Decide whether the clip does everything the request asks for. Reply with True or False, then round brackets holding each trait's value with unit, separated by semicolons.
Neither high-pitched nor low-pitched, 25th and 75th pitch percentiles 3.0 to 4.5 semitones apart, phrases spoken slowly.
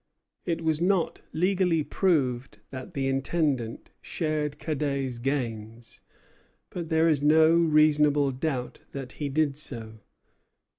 True (145 Hz; 3.3 semitones; 115 wpm)